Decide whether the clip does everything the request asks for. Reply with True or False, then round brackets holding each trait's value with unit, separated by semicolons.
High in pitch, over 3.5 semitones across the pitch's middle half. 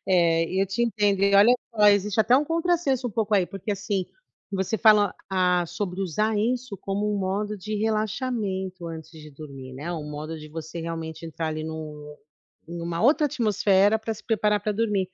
True (195 Hz; 4.4 semitones)